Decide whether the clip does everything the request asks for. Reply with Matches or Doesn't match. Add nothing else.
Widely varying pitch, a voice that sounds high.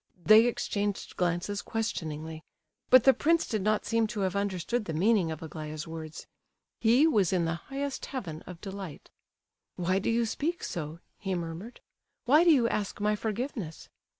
Matches